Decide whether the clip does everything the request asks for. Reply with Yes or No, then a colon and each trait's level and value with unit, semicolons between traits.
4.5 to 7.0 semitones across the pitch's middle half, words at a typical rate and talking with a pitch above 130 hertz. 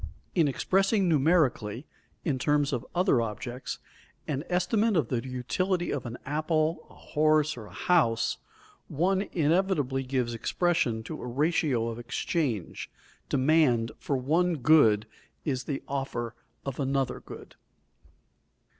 No: average, 5.0 semitones; slow, 130 wpm; medium, 140 Hz